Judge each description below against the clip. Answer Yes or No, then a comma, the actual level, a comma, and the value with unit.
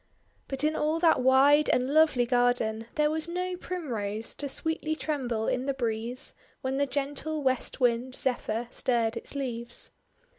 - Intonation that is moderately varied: Yes, average, 4.0 semitones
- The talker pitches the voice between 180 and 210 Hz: No, very high, 265 Hz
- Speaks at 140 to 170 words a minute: Yes, average, 155 wpm